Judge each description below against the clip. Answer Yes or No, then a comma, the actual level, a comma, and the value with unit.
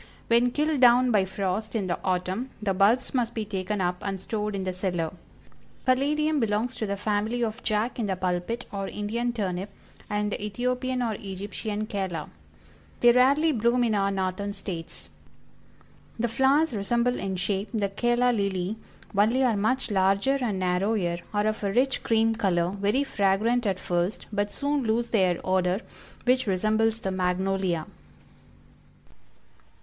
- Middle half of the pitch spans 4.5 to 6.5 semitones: No, average, 3.9 semitones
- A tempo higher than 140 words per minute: Yes, average, 160 wpm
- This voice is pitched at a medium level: No, high, 210 Hz